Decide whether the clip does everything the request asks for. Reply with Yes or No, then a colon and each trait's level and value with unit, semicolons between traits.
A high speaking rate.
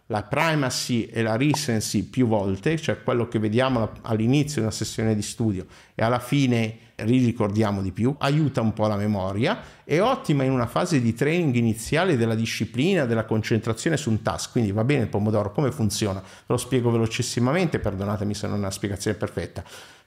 Yes: fast, 180 wpm